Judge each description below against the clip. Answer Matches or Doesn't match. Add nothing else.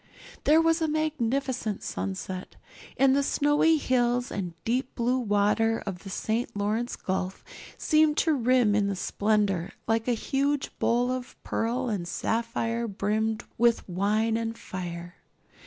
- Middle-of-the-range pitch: Doesn't match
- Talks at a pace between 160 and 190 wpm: Doesn't match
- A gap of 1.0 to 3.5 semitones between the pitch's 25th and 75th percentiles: Doesn't match